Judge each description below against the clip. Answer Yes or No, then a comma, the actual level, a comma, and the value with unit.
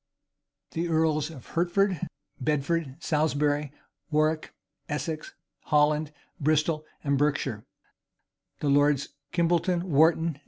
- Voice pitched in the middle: Yes, medium, 155 Hz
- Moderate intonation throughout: No, narrow, 2.1 semitones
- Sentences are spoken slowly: Yes, slow, 90 wpm